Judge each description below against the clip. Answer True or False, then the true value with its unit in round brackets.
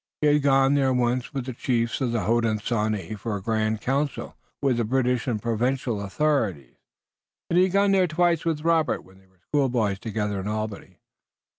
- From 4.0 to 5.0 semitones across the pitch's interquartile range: True (4.7 semitones)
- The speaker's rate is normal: True (180 wpm)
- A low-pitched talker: True (120 Hz)